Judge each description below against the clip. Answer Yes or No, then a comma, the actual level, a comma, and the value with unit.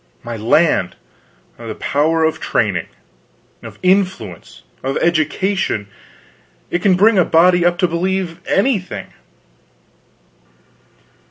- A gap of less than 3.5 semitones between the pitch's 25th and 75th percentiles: No, average, 4.1 semitones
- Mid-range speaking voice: Yes, medium, 170 Hz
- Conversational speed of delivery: No, slow, 100 wpm